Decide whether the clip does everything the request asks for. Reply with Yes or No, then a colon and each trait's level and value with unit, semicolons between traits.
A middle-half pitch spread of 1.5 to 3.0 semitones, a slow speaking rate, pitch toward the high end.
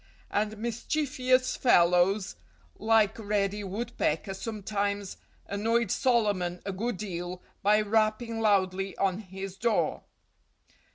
Yes: average, 2.7 semitones; slow, 100 wpm; high, 205 Hz